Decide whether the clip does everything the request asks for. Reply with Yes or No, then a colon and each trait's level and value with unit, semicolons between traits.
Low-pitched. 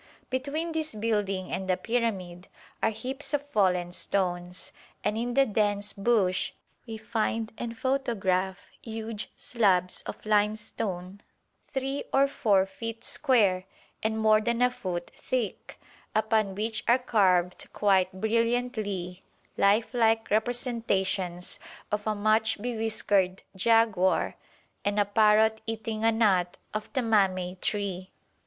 No: high, 215 Hz